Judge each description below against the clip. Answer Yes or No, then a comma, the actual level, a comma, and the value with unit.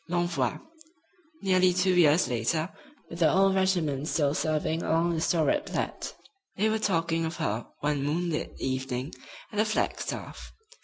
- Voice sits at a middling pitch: Yes, medium, 165 Hz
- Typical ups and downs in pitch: Yes, average, 3.7 semitones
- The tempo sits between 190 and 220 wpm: No, average, 145 wpm